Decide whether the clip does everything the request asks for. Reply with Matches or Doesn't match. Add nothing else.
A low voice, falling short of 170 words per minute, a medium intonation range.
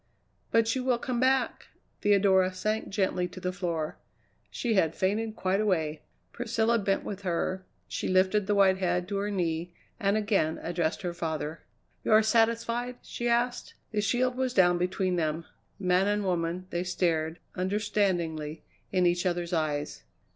Doesn't match